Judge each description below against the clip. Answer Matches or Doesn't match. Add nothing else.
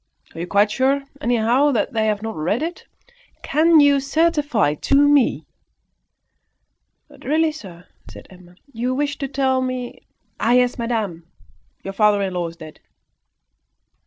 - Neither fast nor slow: Matches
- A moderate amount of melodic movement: Doesn't match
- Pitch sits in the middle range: Doesn't match